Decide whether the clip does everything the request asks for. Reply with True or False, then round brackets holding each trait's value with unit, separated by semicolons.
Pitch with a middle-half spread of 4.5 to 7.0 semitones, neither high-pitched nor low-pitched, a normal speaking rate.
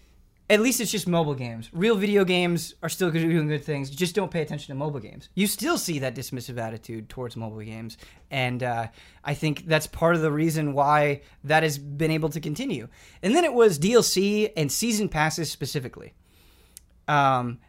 True (5.3 semitones; 155 Hz; 195 wpm)